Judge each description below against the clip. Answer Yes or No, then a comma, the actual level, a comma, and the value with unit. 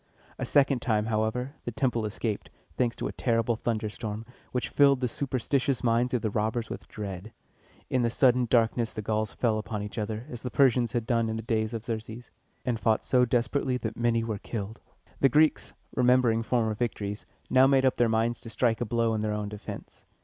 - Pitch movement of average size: No, narrow, 2.3 semitones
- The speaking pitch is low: Yes, low, 115 Hz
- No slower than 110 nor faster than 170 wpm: No, average, 200 wpm